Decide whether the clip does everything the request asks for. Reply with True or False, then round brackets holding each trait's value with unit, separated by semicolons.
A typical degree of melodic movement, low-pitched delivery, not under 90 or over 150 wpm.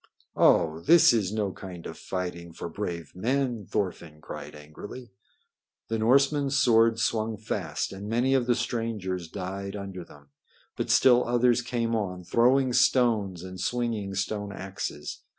True (4.6 semitones; 105 Hz; 145 wpm)